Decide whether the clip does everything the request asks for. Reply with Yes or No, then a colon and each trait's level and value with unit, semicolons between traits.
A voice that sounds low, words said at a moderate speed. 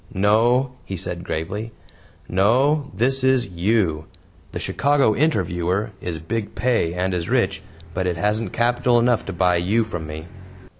Yes: low, 105 Hz; average, 150 wpm